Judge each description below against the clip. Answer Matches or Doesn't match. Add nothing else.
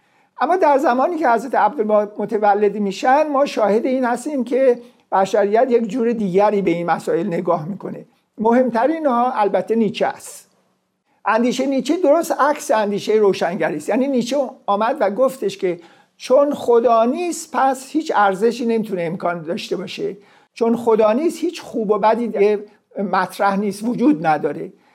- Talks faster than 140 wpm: Matches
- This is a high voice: Matches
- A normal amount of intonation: Matches